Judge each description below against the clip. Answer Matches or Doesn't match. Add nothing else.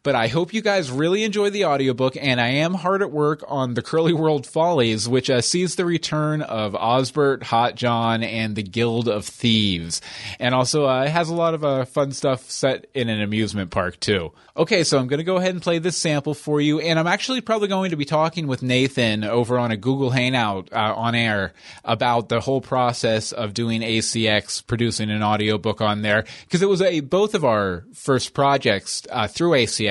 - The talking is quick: Matches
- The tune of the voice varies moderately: Doesn't match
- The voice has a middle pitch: Doesn't match